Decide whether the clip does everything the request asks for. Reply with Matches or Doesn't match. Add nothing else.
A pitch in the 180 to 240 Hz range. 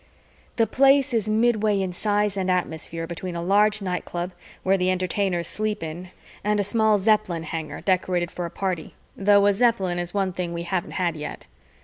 Matches